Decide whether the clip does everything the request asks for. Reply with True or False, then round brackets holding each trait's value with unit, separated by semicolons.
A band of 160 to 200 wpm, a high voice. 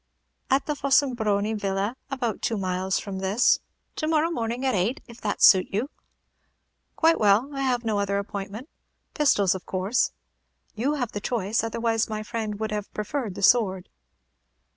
True (165 wpm; 220 Hz)